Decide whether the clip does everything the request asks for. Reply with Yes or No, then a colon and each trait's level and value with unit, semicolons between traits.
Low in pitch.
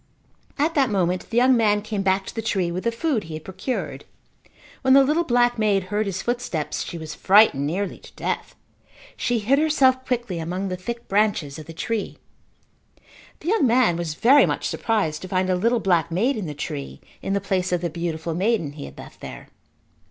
No: high, 200 Hz